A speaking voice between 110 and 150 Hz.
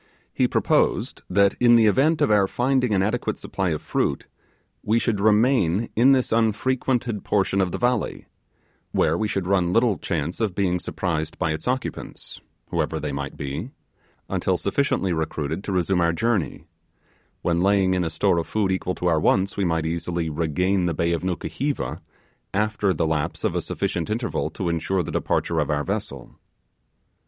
No: very low, 95 Hz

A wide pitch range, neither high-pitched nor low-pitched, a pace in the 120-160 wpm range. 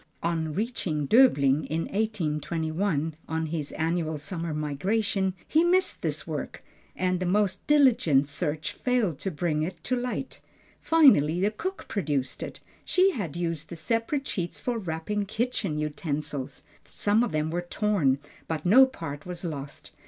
Yes: wide, 5.9 semitones; medium, 175 Hz; average, 150 wpm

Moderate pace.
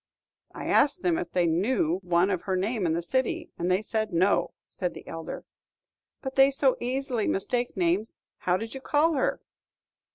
Yes: average, 185 wpm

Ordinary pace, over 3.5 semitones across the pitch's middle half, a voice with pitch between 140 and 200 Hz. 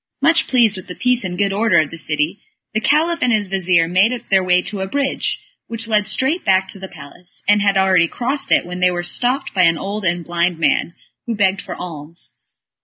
No: fast, 225 wpm; average, 4.3 semitones; high, 190 Hz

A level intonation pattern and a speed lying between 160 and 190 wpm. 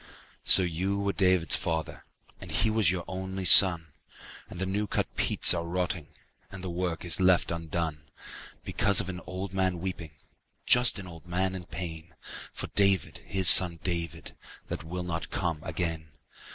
Yes: narrow, 2.1 semitones; average, 165 wpm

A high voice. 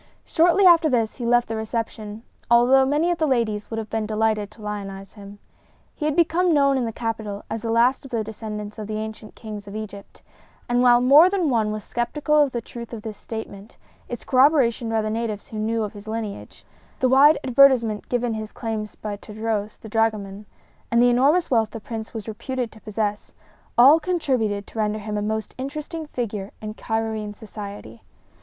Yes: high, 225 Hz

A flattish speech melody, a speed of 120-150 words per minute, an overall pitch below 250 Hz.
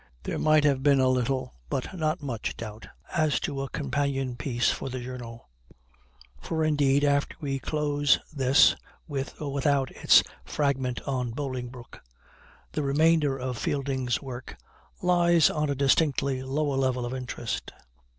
Yes: narrow, 2.2 semitones; average, 145 wpm; low, 135 Hz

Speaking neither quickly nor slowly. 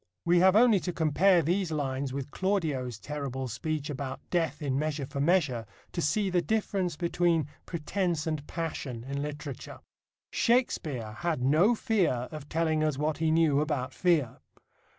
Yes: average, 155 wpm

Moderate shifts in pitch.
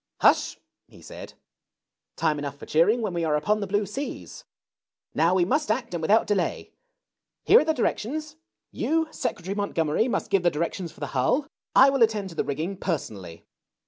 No: wide, 6.4 semitones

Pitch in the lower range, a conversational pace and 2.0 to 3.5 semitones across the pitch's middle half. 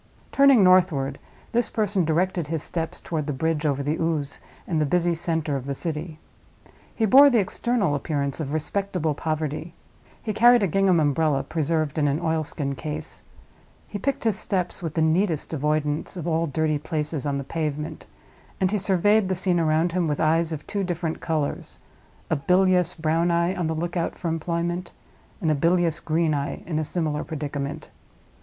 No: medium, 160 Hz; average, 175 wpm; average, 3.0 semitones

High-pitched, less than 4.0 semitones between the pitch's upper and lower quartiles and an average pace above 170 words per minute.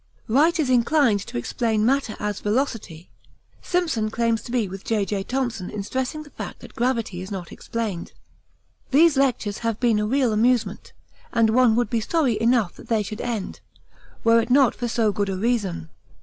Yes: high, 230 Hz; average, 3.4 semitones; average, 180 wpm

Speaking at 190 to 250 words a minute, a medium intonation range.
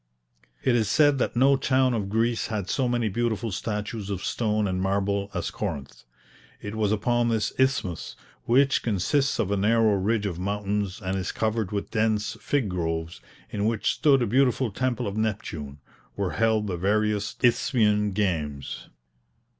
No: average, 160 wpm; average, 3.3 semitones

